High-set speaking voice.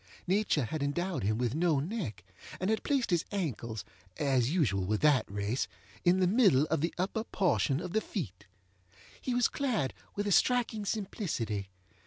No: medium, 170 Hz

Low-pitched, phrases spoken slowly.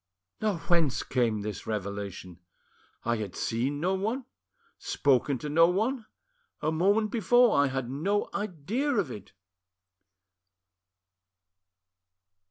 No: medium, 155 Hz; slow, 110 wpm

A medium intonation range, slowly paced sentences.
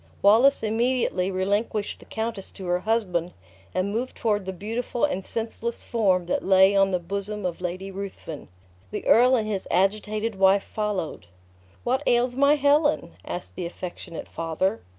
No: average, 3.6 semitones; average, 155 wpm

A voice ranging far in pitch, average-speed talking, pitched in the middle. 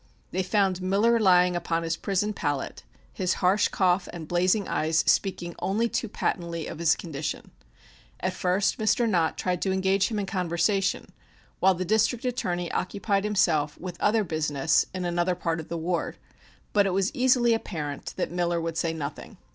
No: average, 3.1 semitones; average, 170 wpm; medium, 180 Hz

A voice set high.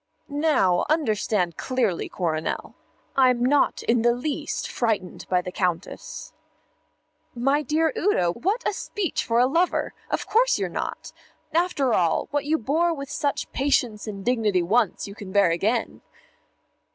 Yes: high, 245 Hz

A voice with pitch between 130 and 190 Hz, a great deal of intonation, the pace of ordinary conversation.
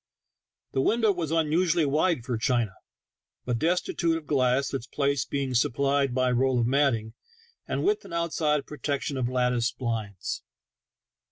No: medium, 140 Hz; average, 4.1 semitones; average, 150 wpm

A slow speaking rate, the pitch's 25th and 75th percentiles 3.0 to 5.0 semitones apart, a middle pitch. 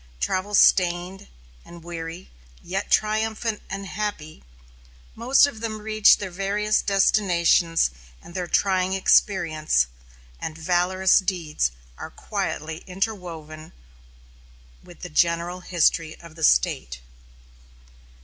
Yes: slow, 105 wpm; average, 3.5 semitones; medium, 180 Hz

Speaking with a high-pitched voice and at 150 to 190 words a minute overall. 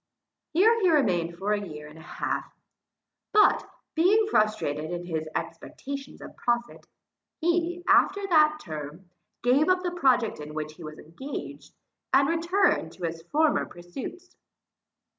No: high, 245 Hz; average, 140 wpm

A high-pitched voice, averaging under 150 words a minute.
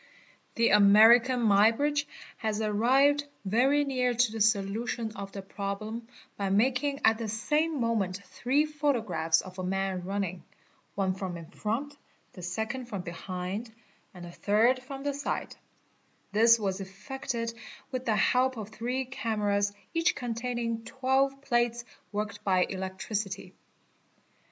Yes: high, 225 Hz; average, 140 wpm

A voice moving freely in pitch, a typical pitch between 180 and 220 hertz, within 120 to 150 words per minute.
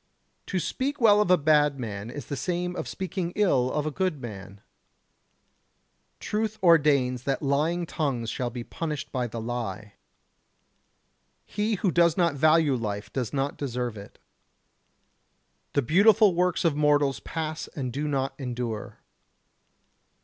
No: wide, 5.8 semitones; medium, 145 Hz; average, 140 wpm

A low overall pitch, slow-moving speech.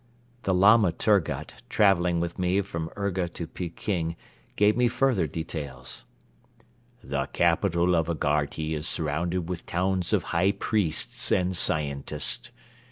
Yes: very low, 85 Hz; slow, 125 wpm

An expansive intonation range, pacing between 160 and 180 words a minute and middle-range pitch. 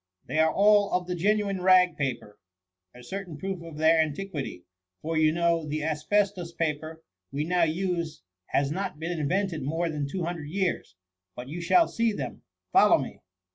No: average, 3.5 semitones; average, 175 wpm; medium, 165 Hz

